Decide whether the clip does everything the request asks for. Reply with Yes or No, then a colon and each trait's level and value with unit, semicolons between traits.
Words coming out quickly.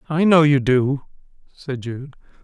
No: average, 150 wpm